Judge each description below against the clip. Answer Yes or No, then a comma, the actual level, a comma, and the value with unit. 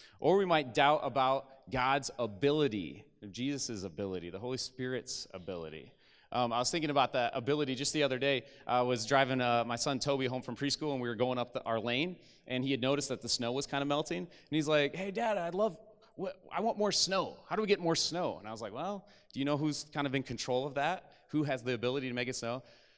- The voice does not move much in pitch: No, average, 3.6 semitones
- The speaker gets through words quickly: Yes, fast, 245 wpm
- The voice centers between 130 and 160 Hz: Yes, medium, 140 Hz